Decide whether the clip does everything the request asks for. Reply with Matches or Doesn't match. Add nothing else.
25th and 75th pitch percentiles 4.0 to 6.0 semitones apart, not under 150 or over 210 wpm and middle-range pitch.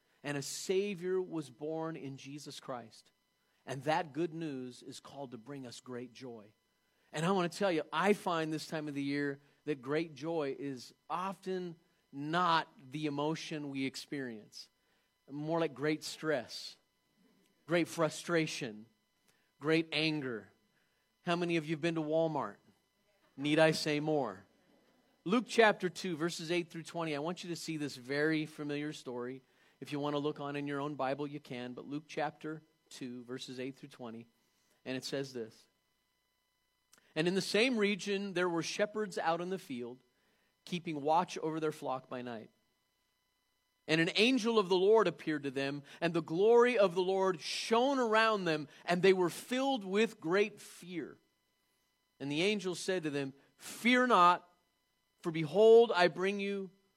Matches